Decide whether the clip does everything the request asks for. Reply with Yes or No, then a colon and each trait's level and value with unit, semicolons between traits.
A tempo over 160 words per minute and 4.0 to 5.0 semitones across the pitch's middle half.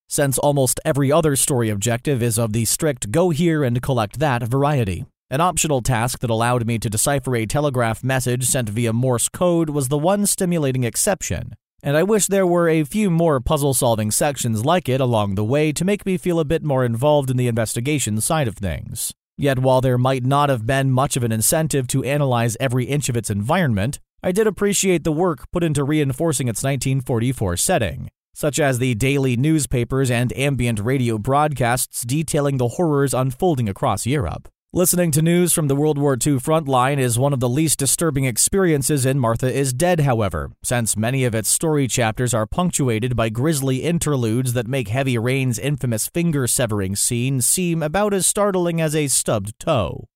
Yes: average, 190 wpm; average, 4.5 semitones